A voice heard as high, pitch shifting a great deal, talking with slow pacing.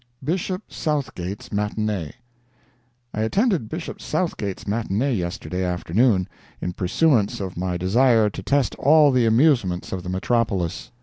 No: low, 110 Hz; wide, 6.6 semitones; slow, 125 wpm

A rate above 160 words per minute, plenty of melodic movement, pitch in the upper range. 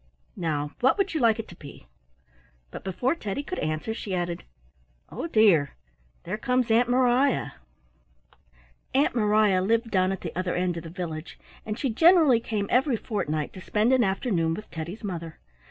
Yes: average, 170 wpm; wide, 5.9 semitones; high, 210 Hz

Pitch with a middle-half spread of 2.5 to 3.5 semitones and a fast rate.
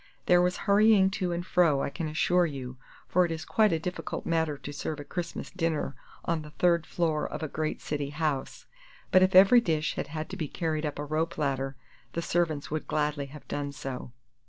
Yes: average, 3.2 semitones; fast, 210 wpm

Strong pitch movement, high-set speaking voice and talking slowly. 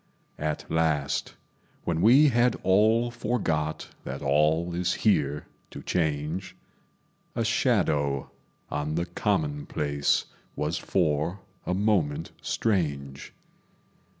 No: wide, 6.2 semitones; very low, 85 Hz; slow, 95 wpm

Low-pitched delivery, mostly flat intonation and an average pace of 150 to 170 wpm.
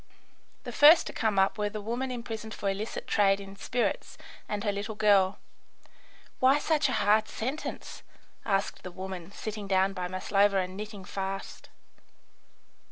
No: high, 205 Hz; narrow, 2.3 semitones; average, 155 wpm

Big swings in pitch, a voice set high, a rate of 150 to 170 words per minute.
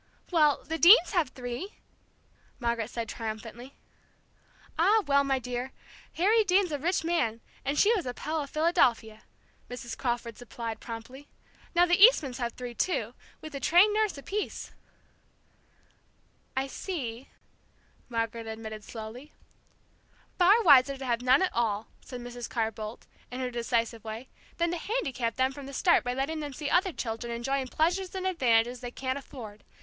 Yes: wide, 5.9 semitones; very high, 260 Hz; average, 160 wpm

